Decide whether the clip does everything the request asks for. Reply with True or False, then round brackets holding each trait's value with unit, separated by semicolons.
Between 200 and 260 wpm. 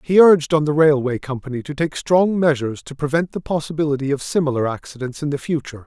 True (205 wpm)